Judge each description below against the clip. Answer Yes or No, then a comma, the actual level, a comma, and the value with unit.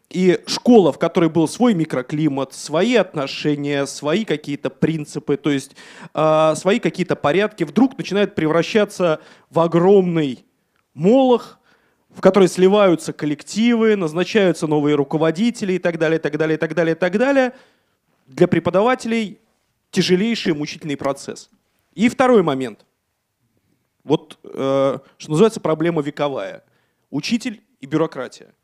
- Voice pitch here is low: No, medium, 170 Hz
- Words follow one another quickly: No, average, 125 wpm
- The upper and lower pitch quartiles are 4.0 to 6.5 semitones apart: Yes, wide, 5.4 semitones